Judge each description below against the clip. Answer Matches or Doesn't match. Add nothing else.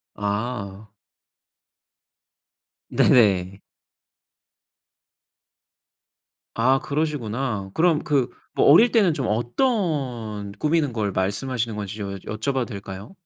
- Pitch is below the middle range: Matches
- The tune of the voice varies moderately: Doesn't match